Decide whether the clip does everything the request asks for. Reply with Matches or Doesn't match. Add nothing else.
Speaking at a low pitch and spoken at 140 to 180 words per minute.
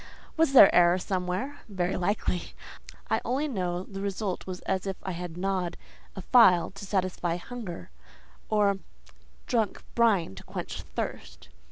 Doesn't match